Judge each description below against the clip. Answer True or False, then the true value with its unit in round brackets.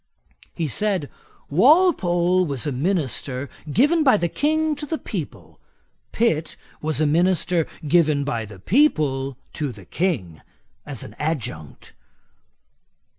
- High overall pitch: False (160 Hz)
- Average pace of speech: False (125 wpm)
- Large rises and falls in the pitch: True (6.5 semitones)